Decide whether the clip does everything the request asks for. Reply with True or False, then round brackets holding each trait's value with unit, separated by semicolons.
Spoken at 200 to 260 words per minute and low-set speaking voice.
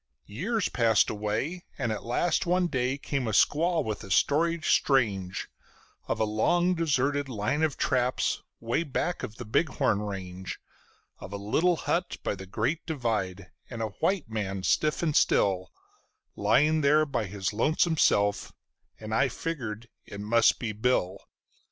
False (155 wpm; 120 Hz)